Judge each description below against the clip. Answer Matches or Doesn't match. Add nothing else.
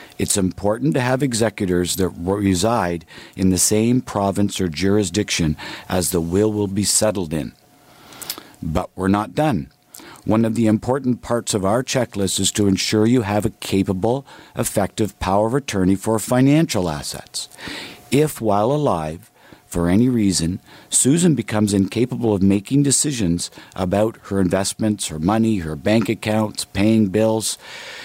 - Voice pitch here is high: Doesn't match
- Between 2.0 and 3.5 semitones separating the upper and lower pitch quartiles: Matches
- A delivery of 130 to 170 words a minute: Matches